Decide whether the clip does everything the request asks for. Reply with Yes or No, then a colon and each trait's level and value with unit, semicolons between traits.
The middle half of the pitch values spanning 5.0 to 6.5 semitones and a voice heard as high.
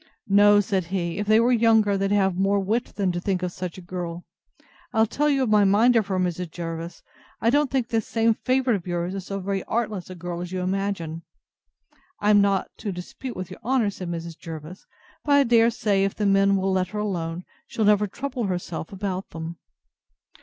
No: average, 3.4 semitones; high, 195 Hz